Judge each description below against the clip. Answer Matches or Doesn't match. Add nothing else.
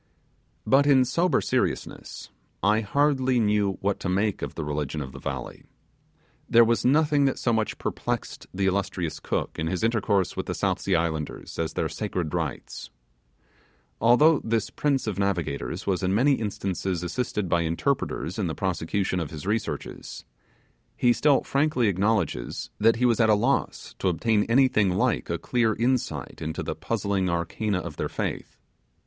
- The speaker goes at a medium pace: Matches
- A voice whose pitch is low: Matches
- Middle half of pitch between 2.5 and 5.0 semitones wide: Doesn't match